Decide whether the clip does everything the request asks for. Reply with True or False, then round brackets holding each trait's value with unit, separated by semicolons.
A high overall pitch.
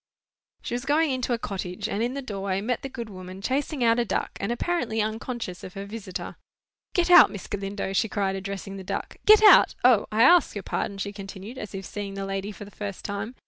True (205 Hz)